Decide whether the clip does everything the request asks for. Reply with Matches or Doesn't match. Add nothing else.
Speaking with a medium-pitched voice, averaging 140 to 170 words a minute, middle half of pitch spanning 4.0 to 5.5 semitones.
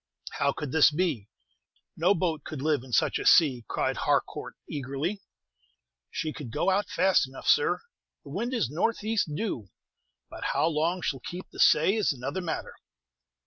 Matches